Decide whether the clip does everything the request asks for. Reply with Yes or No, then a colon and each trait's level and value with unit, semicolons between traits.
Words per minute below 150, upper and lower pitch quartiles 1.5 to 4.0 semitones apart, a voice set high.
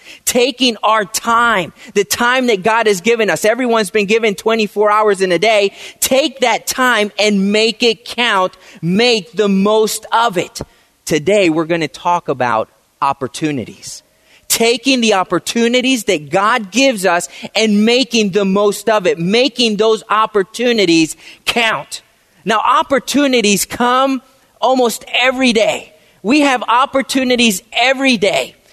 Yes: slow, 135 wpm; average, 3.6 semitones; high, 220 Hz